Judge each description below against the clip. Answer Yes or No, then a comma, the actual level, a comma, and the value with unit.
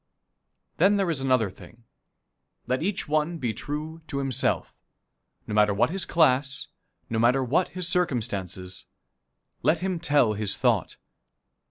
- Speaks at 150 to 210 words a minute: No, average, 140 wpm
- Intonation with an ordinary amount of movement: No, wide, 6.7 semitones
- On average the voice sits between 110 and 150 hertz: Yes, low, 135 Hz